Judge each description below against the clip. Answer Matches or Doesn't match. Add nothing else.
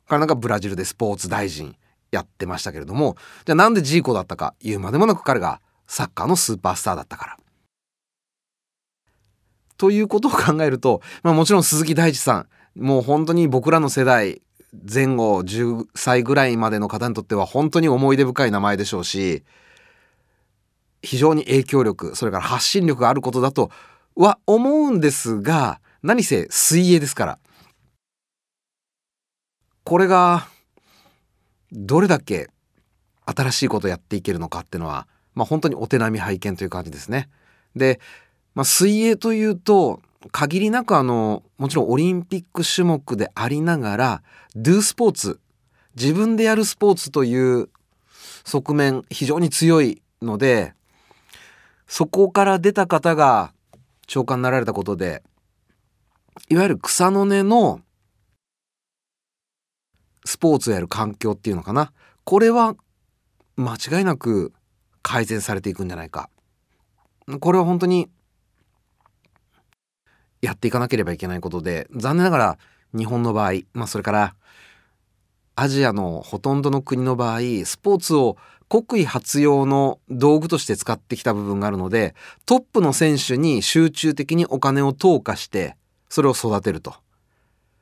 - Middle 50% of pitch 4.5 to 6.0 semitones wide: Doesn't match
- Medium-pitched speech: Doesn't match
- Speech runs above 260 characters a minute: Matches